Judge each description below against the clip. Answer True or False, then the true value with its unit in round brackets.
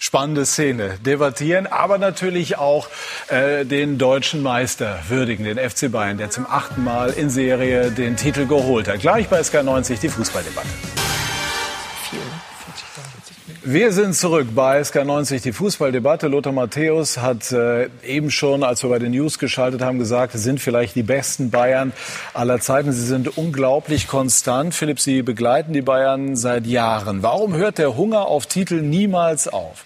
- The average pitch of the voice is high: False (135 Hz)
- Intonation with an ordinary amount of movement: True (3.2 semitones)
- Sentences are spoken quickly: False (155 wpm)